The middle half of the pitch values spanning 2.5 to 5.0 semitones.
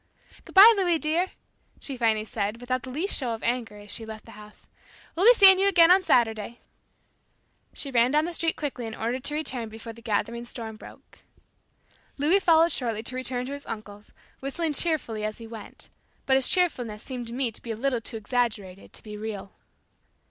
No: wide, 5.5 semitones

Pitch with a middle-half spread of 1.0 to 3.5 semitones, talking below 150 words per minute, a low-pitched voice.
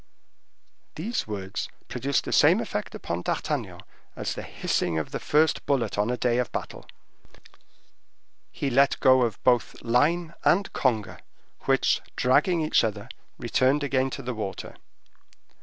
No: average, 4.4 semitones; average, 140 wpm; low, 130 Hz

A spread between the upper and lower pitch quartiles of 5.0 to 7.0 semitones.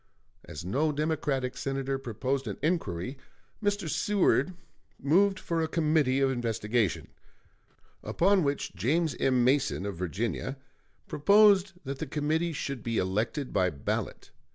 Yes: average, 5.3 semitones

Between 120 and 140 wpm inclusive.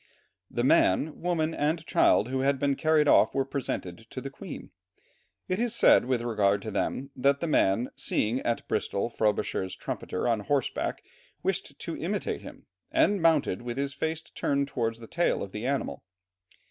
No: average, 170 wpm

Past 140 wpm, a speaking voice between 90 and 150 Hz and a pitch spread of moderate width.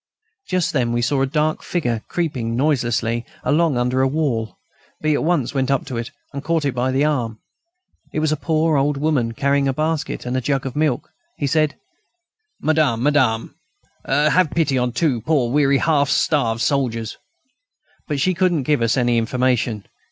Yes: average, 180 wpm; medium, 140 Hz; average, 4.0 semitones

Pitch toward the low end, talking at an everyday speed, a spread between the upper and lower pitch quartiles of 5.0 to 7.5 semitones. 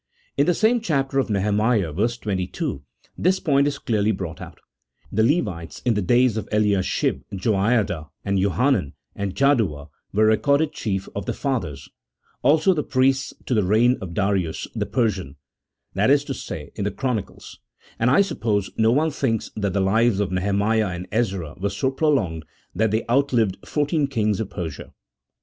Yes: low, 110 Hz; average, 180 wpm; wide, 5.5 semitones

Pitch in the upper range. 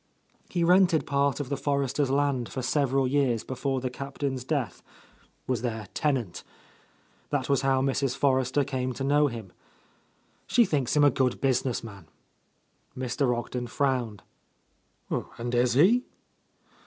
No: low, 135 Hz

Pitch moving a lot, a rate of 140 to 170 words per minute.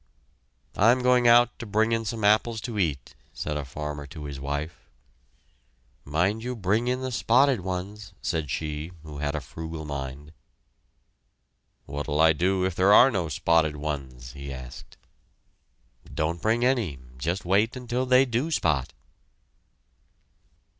Yes: wide, 7.5 semitones; average, 145 wpm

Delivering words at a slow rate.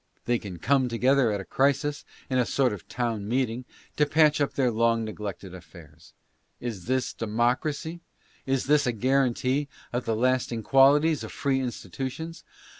No: average, 160 wpm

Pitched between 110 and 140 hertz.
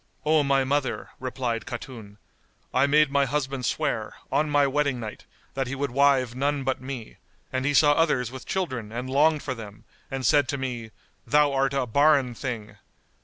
Yes: low, 135 Hz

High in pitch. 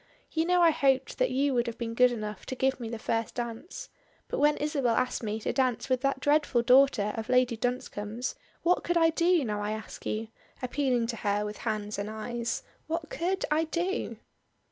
Yes: very high, 250 Hz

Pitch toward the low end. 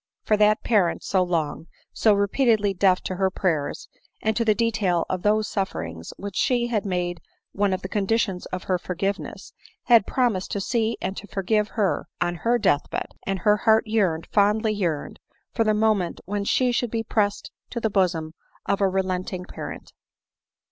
No: high, 200 Hz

